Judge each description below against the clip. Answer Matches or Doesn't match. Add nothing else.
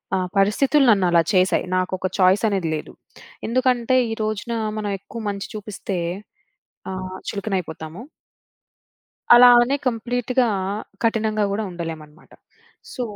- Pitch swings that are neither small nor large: Matches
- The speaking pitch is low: Doesn't match